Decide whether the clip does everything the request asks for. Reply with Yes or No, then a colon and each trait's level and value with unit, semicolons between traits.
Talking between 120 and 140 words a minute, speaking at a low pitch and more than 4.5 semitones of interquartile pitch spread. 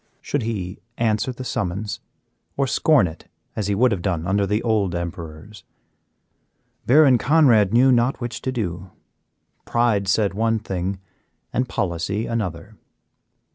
No: slow, 135 wpm; low, 105 Hz; average, 4.1 semitones